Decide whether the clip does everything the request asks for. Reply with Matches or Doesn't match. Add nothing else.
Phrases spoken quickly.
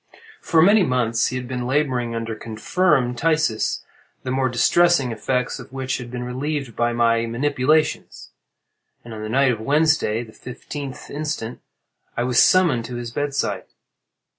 Doesn't match